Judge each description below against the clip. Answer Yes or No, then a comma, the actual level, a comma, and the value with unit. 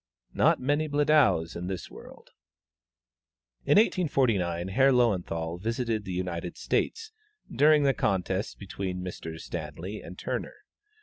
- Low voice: Yes, low, 100 Hz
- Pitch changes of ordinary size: No, wide, 7.5 semitones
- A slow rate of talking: Yes, slow, 120 wpm